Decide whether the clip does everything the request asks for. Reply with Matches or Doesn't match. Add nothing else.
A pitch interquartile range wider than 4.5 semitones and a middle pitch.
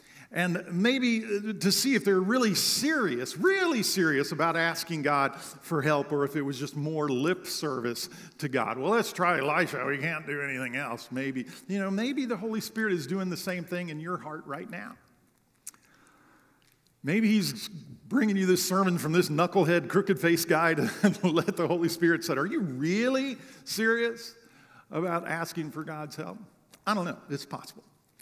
Matches